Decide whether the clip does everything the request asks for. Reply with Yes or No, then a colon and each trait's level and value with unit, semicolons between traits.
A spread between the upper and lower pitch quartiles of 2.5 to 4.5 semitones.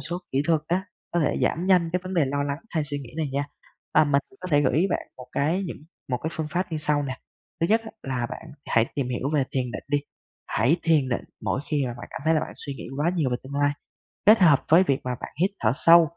Yes: average, 3.8 semitones